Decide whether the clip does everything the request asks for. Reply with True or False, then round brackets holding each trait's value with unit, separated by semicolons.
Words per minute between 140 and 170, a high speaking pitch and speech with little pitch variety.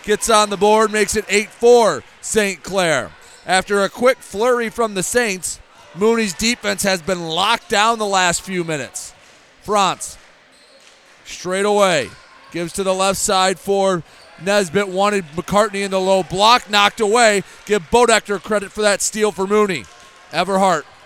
True (150 wpm; 200 Hz; 2.2 semitones)